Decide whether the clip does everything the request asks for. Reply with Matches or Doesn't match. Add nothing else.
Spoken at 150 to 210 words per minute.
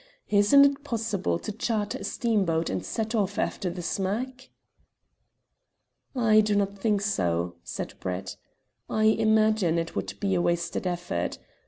Doesn't match